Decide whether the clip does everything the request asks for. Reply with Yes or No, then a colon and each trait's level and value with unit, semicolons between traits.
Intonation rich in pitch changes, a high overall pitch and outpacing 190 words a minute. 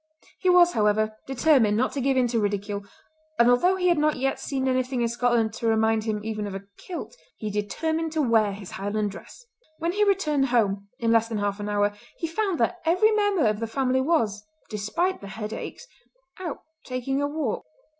Yes: wide, 6.9 semitones; high, 240 Hz; average, 200 wpm